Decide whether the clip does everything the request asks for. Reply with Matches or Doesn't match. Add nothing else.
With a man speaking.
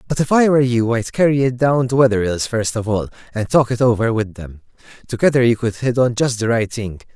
Matches